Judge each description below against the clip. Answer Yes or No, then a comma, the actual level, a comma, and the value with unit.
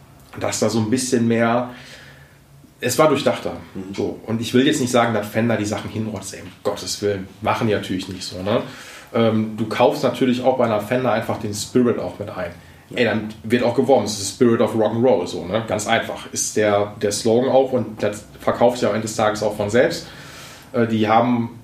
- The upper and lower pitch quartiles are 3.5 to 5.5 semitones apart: No, narrow, 2.6 semitones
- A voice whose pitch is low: Yes, low, 110 Hz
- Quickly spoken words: Yes, fast, 215 wpm